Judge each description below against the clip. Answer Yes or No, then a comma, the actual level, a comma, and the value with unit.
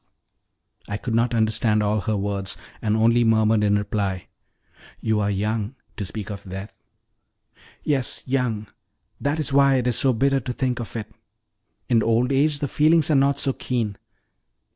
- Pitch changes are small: No, average, 4.1 semitones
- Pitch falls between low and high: No, low, 115 Hz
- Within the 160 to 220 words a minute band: Yes, average, 165 wpm